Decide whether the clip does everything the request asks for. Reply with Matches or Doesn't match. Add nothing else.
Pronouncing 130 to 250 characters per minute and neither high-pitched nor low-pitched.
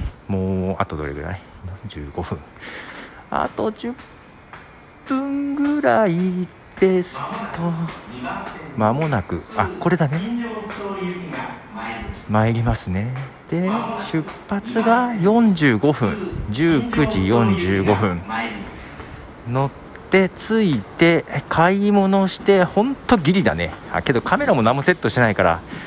Matches